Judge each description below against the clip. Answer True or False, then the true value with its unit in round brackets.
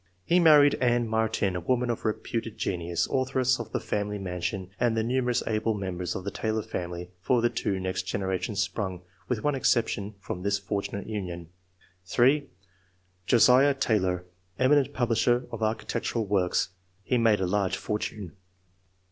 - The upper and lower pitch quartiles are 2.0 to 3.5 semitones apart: False (4.4 semitones)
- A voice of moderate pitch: False (110 Hz)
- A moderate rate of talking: True (155 wpm)